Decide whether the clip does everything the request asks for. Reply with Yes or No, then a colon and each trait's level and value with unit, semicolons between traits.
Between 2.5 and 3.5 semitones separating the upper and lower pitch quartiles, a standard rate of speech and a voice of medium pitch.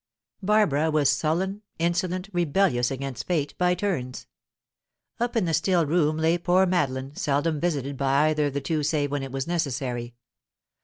No: average, 4.1 semitones; average, 160 wpm; medium, 155 Hz